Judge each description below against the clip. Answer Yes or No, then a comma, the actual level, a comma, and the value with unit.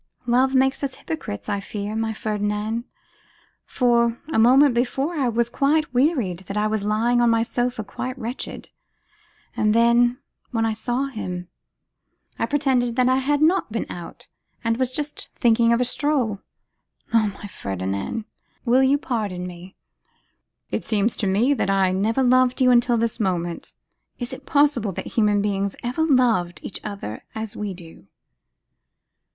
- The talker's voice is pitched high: Yes, high, 230 Hz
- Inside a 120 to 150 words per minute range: No, average, 160 wpm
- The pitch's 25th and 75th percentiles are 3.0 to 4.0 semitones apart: Yes, average, 3.7 semitones